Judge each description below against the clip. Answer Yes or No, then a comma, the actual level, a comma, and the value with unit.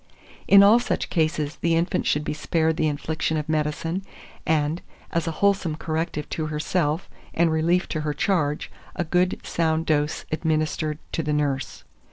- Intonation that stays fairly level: Yes, narrow, 1.9 semitones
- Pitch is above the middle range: No, medium, 160 Hz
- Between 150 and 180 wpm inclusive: Yes, average, 165 wpm